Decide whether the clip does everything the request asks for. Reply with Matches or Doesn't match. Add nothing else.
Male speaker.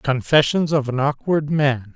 Matches